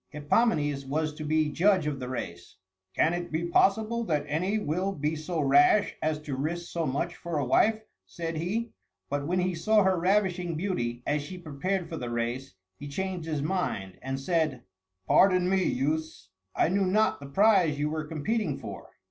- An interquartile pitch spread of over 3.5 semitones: Yes, average, 4.3 semitones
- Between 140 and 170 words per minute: No, average, 185 wpm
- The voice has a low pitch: No, medium, 160 Hz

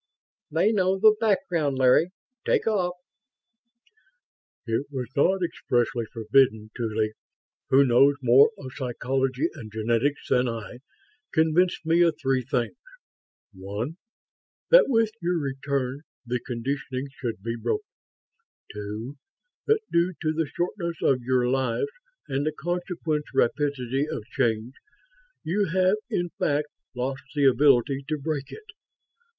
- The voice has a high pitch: No, low, 135 Hz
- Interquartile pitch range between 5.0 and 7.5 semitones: Yes, wide, 5.4 semitones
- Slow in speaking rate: Yes, slow, 125 wpm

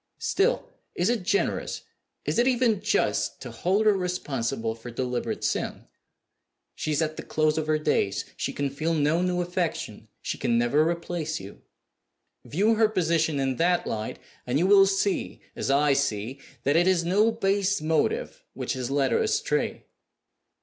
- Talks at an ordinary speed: Yes, average, 170 wpm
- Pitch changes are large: Yes, wide, 5.8 semitones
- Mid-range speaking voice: Yes, medium, 165 Hz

